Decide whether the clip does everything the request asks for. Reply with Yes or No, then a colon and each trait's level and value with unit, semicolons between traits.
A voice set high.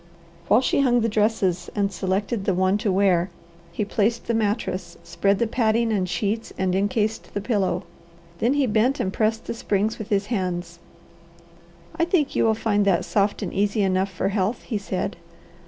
Yes: high, 205 Hz